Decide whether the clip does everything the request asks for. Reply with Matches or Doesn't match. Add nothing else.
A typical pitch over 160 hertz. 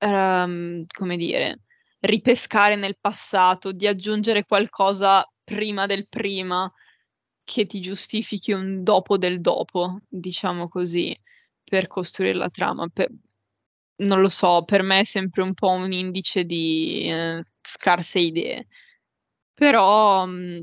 Matches